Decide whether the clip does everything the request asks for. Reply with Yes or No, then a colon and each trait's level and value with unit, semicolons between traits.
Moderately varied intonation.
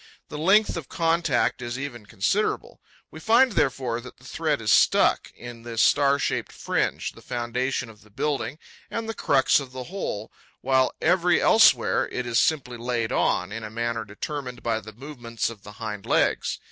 Yes: average, 4.4 semitones